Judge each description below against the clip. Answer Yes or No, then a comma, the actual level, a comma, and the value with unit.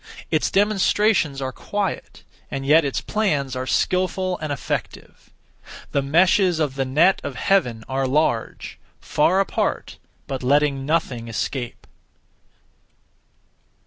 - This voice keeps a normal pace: No, slow, 115 wpm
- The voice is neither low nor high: Yes, medium, 145 Hz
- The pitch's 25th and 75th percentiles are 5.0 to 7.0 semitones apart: Yes, wide, 5.6 semitones